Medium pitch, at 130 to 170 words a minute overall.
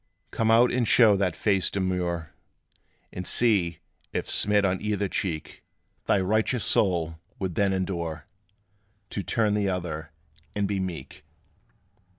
No: very low, 95 Hz; slow, 135 wpm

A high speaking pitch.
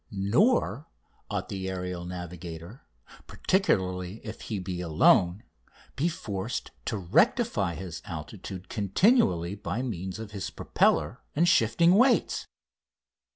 No: very low, 95 Hz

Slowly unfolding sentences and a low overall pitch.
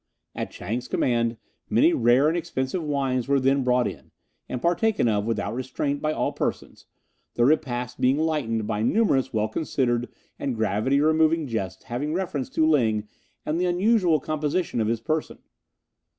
No: average, 160 wpm; low, 130 Hz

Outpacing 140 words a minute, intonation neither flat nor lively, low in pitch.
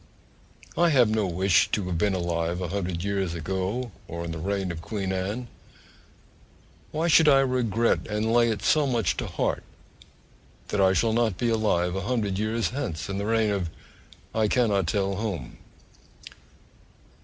Yes: average, 165 wpm; average, 3.9 semitones; low, 100 Hz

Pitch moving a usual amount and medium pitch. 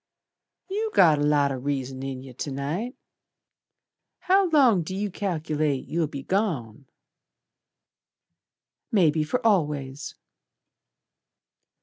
No: wide, 6.4 semitones; medium, 155 Hz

